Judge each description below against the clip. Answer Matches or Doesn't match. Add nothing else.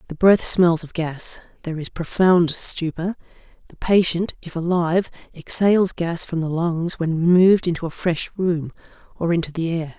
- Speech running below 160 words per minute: Doesn't match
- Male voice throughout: Doesn't match